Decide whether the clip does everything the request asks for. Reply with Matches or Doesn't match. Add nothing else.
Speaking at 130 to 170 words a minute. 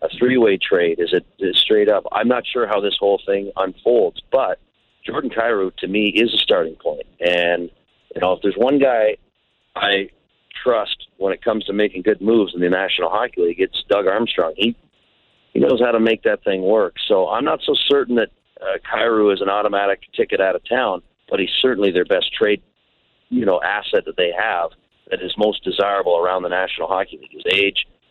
Doesn't match